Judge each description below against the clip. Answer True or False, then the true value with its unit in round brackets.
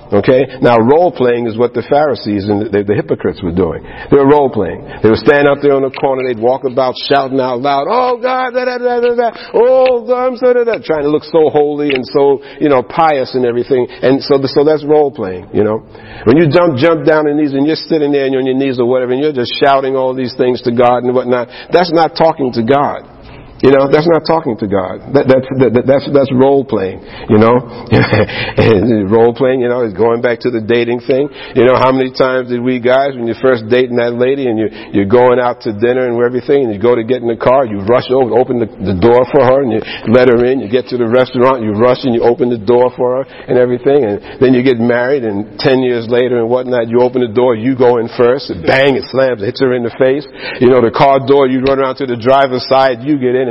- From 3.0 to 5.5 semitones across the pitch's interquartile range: False (2.5 semitones)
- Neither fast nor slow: False (260 wpm)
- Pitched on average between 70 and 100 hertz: False (130 Hz)